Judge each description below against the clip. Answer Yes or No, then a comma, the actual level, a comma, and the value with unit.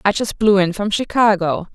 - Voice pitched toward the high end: Yes, high, 200 Hz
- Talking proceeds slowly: No, fast, 205 wpm